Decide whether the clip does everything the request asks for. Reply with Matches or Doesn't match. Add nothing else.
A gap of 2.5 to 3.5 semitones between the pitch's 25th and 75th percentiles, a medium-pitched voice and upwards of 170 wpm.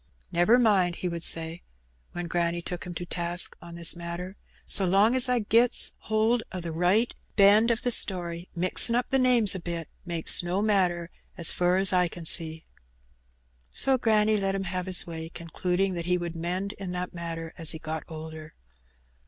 Matches